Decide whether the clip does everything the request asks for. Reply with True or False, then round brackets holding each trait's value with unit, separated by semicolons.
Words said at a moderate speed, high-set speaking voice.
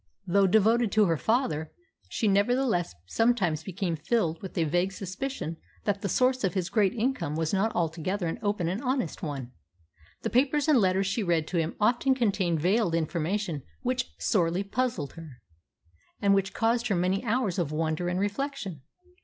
True (170 wpm; 195 Hz)